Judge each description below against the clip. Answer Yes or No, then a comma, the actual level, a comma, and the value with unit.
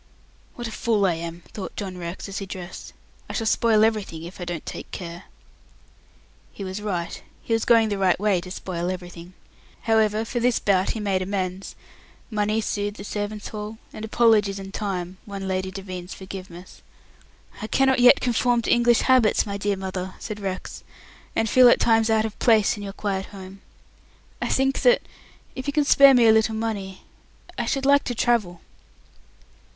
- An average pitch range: Yes, average, 3.1 semitones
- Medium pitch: No, high, 205 Hz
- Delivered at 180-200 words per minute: Yes, average, 185 wpm